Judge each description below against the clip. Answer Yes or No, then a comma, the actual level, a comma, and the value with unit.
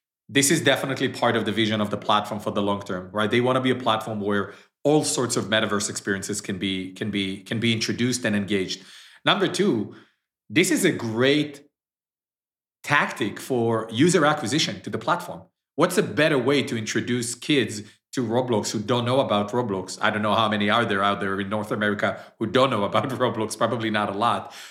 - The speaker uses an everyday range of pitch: Yes, average, 3.3 semitones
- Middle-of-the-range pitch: No, low, 110 Hz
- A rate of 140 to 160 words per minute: No, fast, 205 wpm